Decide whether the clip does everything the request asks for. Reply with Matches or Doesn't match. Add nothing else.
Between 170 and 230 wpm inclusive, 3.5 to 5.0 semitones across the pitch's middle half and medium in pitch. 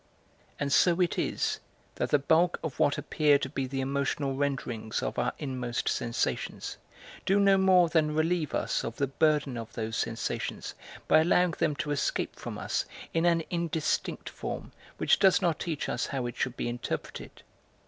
Matches